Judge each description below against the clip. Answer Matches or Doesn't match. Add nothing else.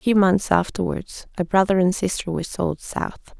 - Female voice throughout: Matches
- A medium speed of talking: Matches